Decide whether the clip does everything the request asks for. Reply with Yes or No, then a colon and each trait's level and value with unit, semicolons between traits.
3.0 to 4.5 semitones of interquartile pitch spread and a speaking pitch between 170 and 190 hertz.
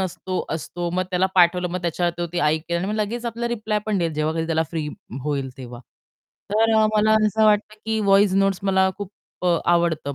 Yes: average, 4.1 semitones; medium, 185 Hz